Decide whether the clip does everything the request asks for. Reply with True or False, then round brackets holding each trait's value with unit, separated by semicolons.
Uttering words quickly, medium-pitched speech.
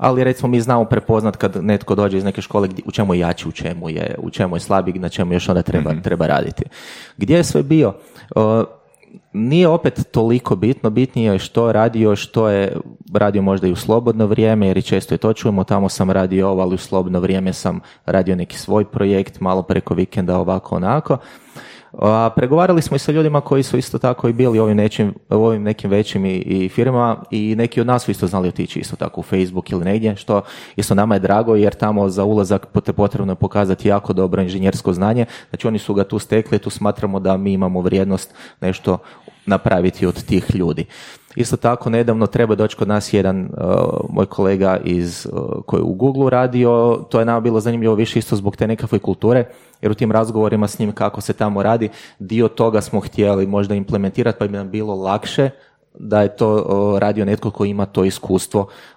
False (200 wpm; 105 Hz)